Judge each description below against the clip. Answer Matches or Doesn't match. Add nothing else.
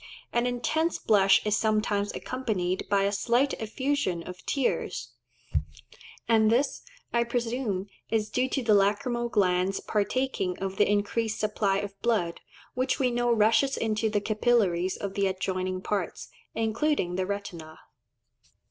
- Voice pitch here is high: Matches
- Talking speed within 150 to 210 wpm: Doesn't match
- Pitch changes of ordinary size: Matches